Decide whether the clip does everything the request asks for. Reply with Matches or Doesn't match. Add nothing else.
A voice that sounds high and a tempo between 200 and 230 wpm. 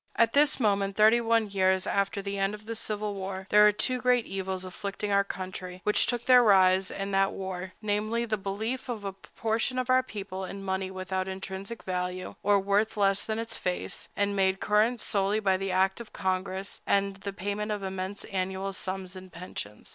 Matches